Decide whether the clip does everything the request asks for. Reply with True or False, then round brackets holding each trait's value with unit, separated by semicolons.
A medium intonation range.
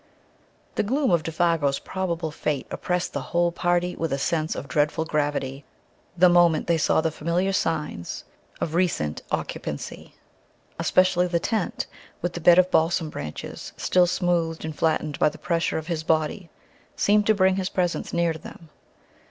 False (2.2 semitones)